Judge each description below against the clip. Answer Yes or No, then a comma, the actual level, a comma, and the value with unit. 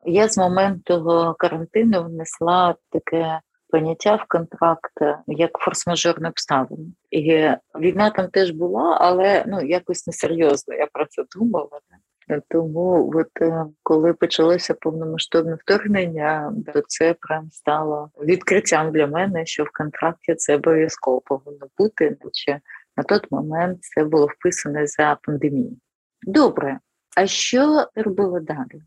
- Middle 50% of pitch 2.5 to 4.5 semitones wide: Yes, average, 2.8 semitones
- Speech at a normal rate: Yes, average, 125 wpm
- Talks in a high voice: No, medium, 165 Hz